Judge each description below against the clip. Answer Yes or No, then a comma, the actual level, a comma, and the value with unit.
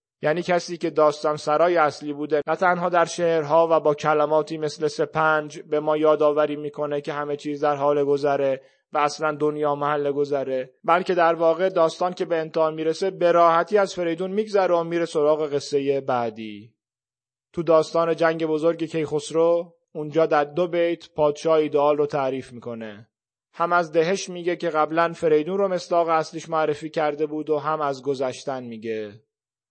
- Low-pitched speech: No, medium, 155 Hz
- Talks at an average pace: No, fast, 165 wpm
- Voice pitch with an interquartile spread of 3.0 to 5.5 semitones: No, narrow, 2.5 semitones